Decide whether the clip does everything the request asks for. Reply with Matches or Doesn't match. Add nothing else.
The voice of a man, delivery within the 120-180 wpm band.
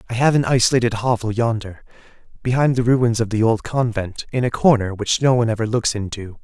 Doesn't match